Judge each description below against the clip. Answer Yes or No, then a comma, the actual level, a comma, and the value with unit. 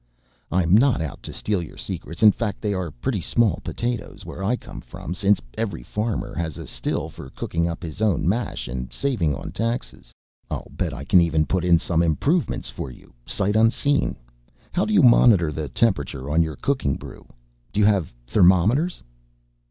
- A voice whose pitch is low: Yes, very low, 95 Hz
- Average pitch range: No, wide, 6.0 semitones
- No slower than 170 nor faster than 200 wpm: Yes, average, 185 wpm